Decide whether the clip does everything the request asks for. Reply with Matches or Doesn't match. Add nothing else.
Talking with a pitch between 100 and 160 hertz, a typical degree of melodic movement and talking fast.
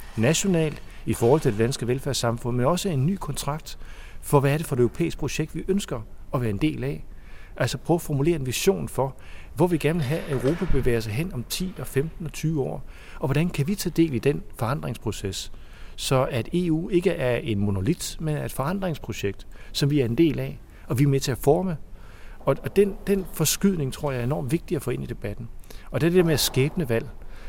Doesn't match